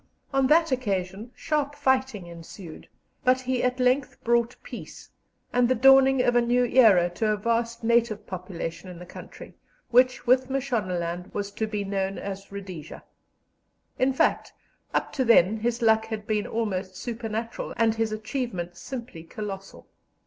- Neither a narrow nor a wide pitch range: Yes, average, 4.4 semitones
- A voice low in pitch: No, high, 225 Hz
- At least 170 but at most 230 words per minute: No, average, 155 wpm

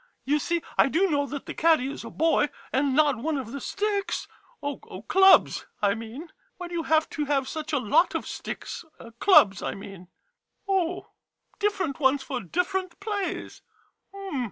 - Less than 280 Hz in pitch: No, very high, 300 Hz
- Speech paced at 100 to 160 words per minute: No, average, 180 wpm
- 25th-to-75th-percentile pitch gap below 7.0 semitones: Yes, average, 5.2 semitones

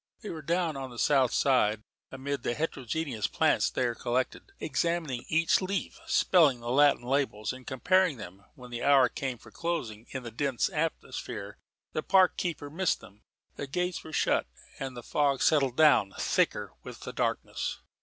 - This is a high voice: No, low, 135 Hz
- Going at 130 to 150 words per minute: No, average, 170 wpm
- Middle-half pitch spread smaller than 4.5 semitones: No, average, 4.8 semitones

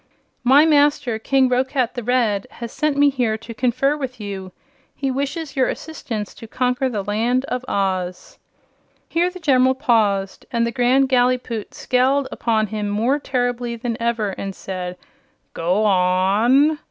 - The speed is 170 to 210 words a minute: No, average, 155 wpm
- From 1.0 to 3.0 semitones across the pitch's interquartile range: No, average, 4.0 semitones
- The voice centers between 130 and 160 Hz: No, high, 245 Hz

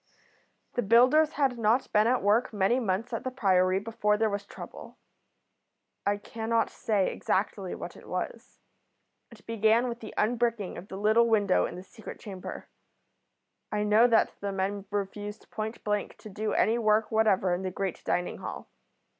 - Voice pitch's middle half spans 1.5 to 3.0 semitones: Yes, narrow, 2.5 semitones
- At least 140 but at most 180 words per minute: Yes, average, 170 wpm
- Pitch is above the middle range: Yes, high, 215 Hz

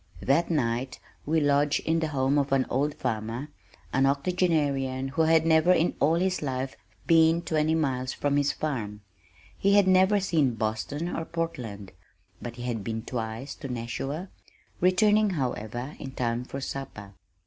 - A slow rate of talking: No, average, 160 wpm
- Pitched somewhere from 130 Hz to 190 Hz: Yes, medium, 140 Hz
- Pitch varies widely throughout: No, average, 4.6 semitones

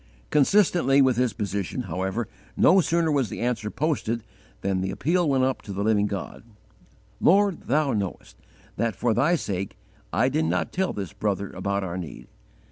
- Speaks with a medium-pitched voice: No, low, 120 Hz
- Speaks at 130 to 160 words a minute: No, average, 175 wpm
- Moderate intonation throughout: No, wide, 7.1 semitones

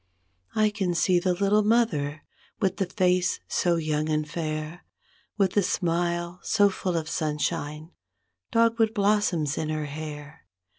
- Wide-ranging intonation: No, average, 4.5 semitones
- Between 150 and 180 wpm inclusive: No, average, 140 wpm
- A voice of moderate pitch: Yes, medium, 175 Hz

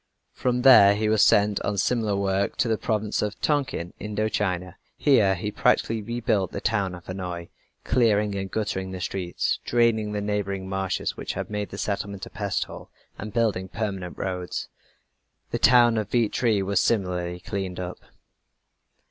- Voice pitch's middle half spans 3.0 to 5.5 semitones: No, narrow, 2.5 semitones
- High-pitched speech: No, low, 100 Hz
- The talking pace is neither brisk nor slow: Yes, average, 165 wpm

